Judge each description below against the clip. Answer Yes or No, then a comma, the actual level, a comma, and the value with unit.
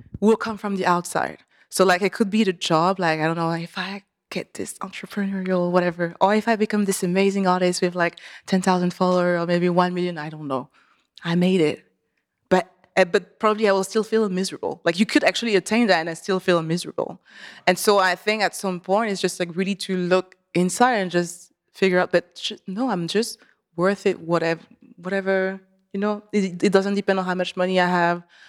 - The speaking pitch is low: No, medium, 185 Hz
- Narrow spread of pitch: Yes, narrow, 2.2 semitones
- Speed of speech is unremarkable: No, fast, 215 wpm